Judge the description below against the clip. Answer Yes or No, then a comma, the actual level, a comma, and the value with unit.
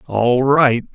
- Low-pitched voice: Yes, low, 125 Hz